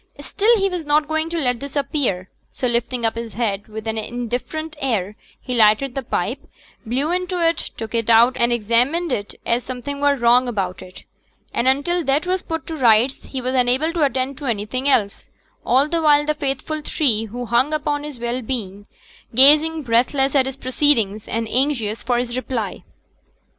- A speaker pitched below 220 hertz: No, very high, 255 Hz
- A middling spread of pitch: Yes, average, 4.2 semitones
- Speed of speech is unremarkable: Yes, average, 190 wpm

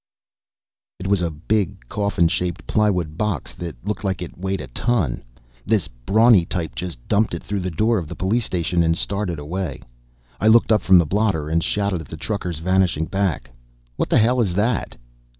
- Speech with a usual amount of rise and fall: Yes, average, 4.0 semitones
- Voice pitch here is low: Yes, very low, 95 Hz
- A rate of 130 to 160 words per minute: No, average, 190 wpm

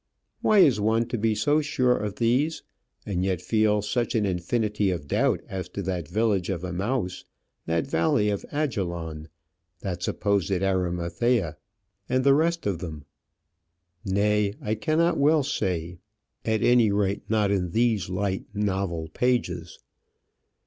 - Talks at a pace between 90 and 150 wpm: Yes, average, 140 wpm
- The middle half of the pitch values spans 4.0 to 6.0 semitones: Yes, average, 4.7 semitones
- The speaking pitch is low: Yes, low, 105 Hz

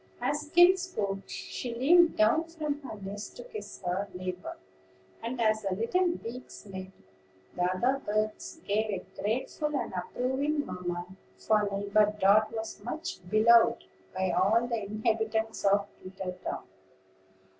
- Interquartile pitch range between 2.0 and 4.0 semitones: No, average, 5.1 semitones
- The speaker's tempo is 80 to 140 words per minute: Yes, slow, 135 wpm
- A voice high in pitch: Yes, high, 215 Hz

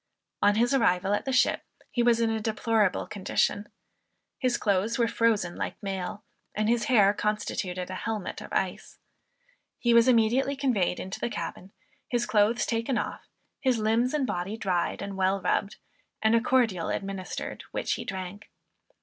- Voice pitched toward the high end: Yes, high, 215 Hz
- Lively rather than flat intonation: No, average, 3.3 semitones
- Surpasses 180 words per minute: No, average, 165 wpm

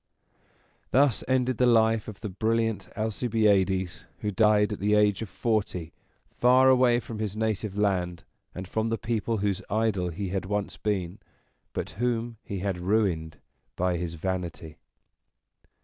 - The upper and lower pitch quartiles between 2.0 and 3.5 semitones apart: Yes, average, 3.2 semitones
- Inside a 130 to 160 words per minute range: Yes, average, 150 wpm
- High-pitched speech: No, low, 105 Hz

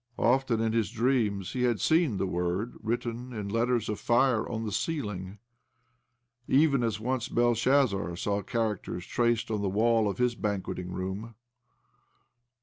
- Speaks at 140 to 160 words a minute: Yes, average, 145 wpm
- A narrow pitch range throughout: No, average, 3.3 semitones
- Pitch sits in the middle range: No, low, 115 Hz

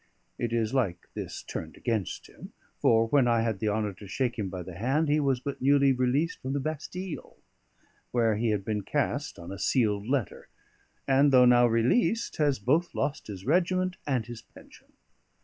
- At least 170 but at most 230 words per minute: Yes, average, 185 wpm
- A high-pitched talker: No, low, 125 Hz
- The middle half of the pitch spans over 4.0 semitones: Yes, average, 4.8 semitones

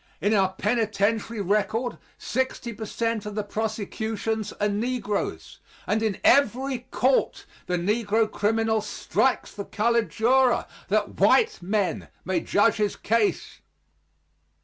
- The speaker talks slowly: Yes, slow, 125 wpm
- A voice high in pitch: Yes, high, 220 Hz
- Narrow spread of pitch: Yes, narrow, 2.1 semitones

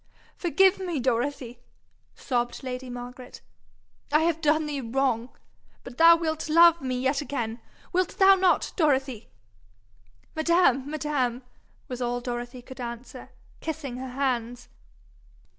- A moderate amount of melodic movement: Yes, average, 4.3 semitones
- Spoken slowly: Yes, slow, 125 wpm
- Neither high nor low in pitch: No, very high, 265 Hz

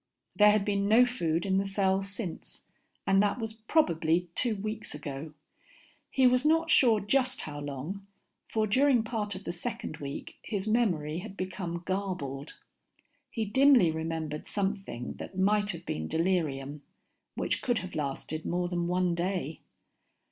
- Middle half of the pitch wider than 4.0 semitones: Yes, average, 4.9 semitones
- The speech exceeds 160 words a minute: No, average, 155 wpm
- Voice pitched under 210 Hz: Yes, high, 190 Hz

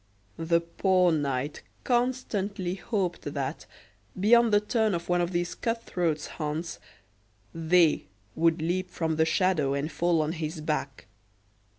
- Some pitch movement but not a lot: Yes, average, 3.1 semitones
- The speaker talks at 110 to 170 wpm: Yes, slow, 135 wpm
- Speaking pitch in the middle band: Yes, medium, 170 Hz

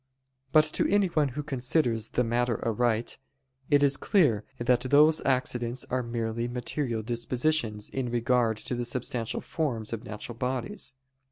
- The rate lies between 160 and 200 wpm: No, average, 145 wpm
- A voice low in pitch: Yes, low, 125 Hz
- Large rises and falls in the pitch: No, average, 3.1 semitones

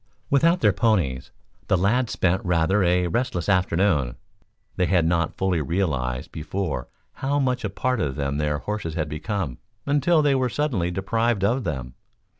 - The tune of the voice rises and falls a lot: Yes, wide, 6.6 semitones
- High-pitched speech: No, very low, 95 Hz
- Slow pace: No, average, 160 wpm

